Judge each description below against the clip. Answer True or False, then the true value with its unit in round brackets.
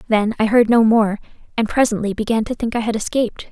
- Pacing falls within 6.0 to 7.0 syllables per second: True (6.3 syllables/s)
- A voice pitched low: False (220 Hz)